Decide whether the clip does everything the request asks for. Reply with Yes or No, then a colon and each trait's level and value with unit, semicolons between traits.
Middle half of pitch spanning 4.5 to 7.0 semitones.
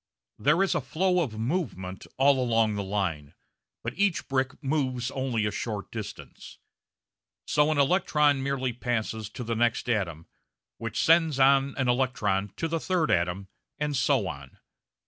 Yes: wide, 5.4 semitones